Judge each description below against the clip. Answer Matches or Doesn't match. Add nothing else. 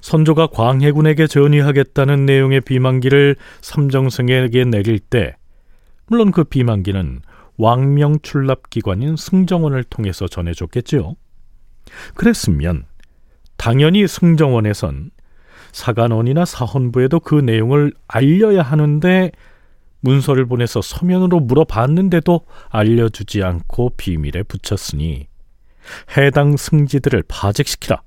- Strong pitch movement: Matches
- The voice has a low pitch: Matches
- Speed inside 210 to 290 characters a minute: Matches